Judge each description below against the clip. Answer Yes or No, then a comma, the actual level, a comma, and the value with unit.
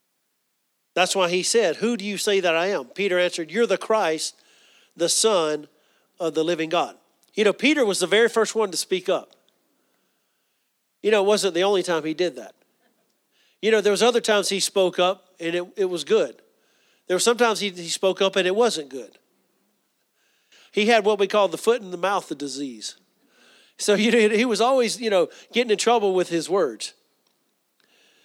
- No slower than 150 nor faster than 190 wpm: No, average, 200 wpm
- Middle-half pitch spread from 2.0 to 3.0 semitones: No, average, 4.0 semitones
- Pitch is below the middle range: No, high, 195 Hz